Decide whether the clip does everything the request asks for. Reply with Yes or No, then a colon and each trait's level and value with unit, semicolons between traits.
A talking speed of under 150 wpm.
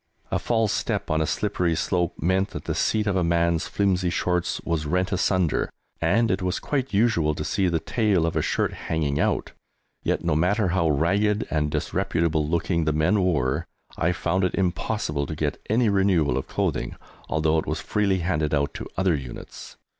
No: average, 190 wpm